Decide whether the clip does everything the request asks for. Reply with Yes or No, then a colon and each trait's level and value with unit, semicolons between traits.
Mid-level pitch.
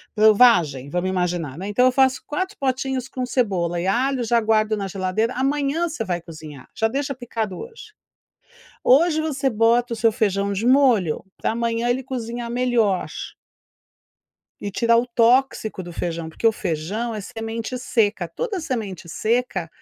No: high, 230 Hz